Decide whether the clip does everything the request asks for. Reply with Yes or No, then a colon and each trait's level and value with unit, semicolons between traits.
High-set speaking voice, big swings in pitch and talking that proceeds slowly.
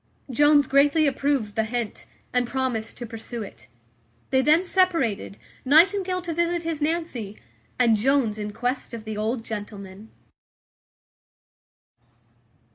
Yes: very high, 255 Hz; wide, 5.8 semitones; slow, 120 wpm